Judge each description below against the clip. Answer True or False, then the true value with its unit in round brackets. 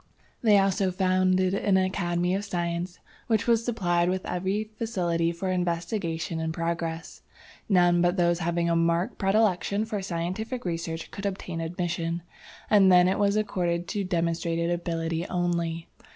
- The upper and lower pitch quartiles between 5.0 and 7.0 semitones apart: False (2.5 semitones)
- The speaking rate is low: False (145 wpm)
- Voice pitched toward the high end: False (175 Hz)